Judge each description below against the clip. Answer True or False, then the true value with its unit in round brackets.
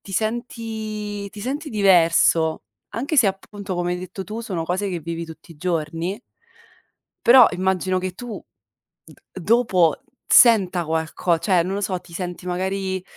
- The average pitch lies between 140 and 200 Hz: True (190 Hz)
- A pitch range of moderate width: True (3.3 semitones)